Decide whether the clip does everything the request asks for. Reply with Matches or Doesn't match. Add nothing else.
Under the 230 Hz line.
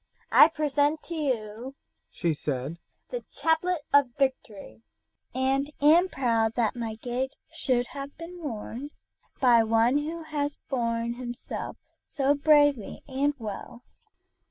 Doesn't match